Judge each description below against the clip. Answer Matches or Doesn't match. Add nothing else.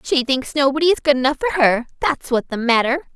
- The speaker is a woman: Matches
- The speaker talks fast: Matches